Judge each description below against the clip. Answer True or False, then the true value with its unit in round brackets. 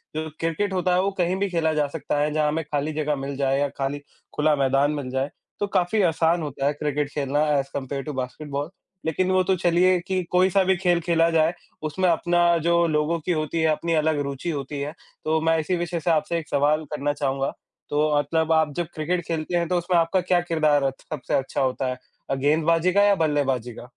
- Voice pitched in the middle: True (155 Hz)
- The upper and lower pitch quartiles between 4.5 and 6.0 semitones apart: False (3.0 semitones)